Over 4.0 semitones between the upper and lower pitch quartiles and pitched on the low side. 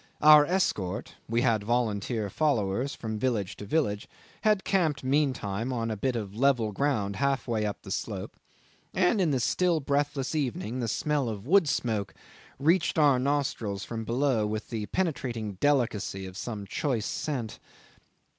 Yes: average, 5.3 semitones; low, 120 Hz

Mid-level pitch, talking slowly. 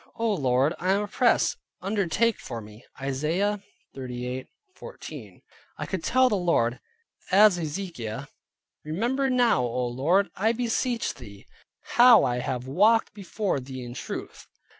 Yes: medium, 180 Hz; slow, 130 wpm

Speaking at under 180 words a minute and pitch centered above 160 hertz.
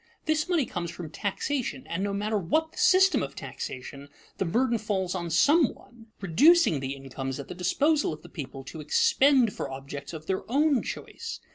No: average, 185 wpm; high, 190 Hz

